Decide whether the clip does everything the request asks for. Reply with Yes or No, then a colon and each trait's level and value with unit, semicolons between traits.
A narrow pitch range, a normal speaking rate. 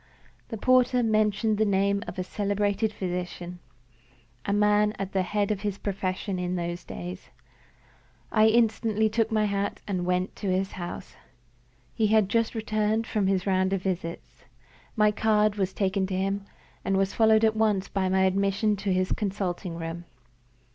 Yes: narrow, 2.3 semitones; average, 165 wpm